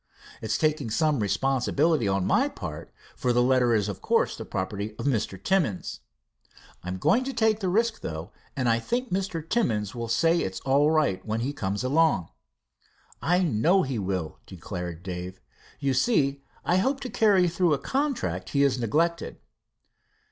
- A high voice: No, low, 135 Hz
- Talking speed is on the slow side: No, average, 170 wpm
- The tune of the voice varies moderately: No, wide, 8.7 semitones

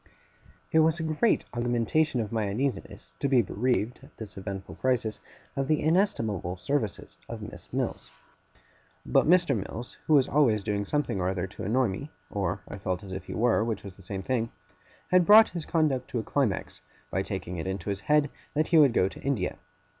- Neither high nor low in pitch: No, low, 115 Hz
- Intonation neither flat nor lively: No, wide, 6.7 semitones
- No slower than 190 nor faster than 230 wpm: Yes, average, 200 wpm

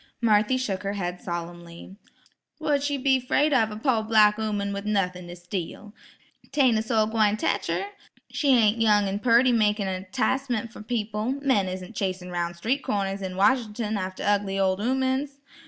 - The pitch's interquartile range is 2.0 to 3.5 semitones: No, average, 4.1 semitones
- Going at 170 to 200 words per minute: Yes, average, 175 wpm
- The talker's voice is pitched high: Yes, high, 210 Hz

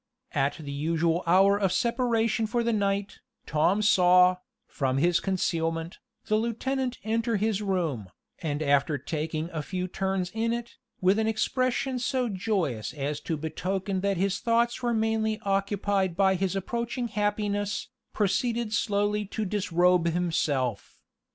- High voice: Yes, high, 195 Hz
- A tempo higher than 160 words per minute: No, average, 140 wpm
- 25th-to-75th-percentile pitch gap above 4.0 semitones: Yes, average, 4.7 semitones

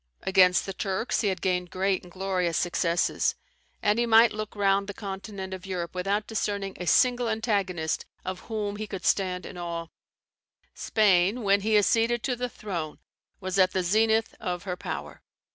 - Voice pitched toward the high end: Yes, high, 195 Hz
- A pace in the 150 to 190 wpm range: Yes, average, 175 wpm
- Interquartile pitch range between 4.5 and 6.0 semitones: No, average, 2.8 semitones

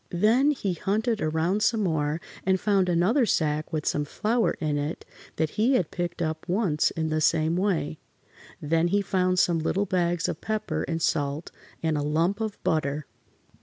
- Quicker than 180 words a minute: No, average, 175 wpm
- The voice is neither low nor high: Yes, medium, 175 Hz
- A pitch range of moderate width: Yes, average, 4.4 semitones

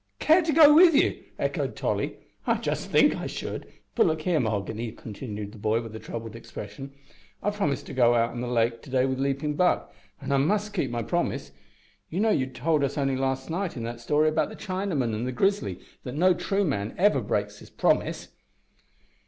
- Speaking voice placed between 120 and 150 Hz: Yes, low, 135 Hz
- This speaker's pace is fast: Yes, fast, 210 wpm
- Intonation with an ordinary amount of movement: No, wide, 7.5 semitones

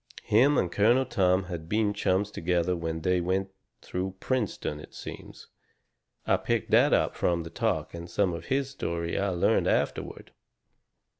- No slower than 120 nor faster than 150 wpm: No, average, 160 wpm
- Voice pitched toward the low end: Yes, very low, 90 Hz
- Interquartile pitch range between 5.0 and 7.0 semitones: No, average, 3.4 semitones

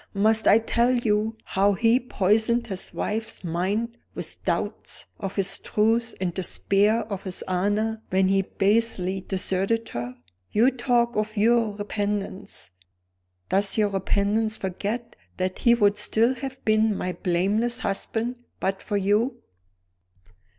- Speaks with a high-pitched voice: Yes, high, 210 Hz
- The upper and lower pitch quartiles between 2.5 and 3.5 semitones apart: Yes, average, 2.8 semitones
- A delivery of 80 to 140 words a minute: Yes, slow, 135 wpm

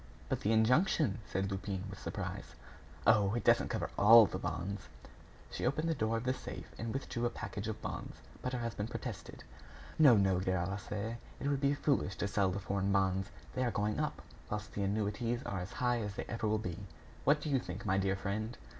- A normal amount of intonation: Yes, average, 3.4 semitones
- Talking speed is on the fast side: Yes, fast, 210 wpm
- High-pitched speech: No, low, 105 Hz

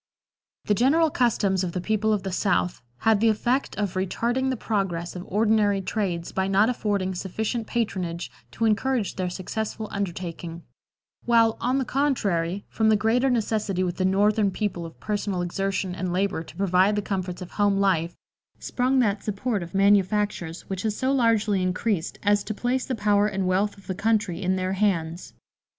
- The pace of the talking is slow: No, average, 175 wpm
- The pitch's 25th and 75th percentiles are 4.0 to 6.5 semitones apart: No, average, 3.0 semitones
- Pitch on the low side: No, high, 200 Hz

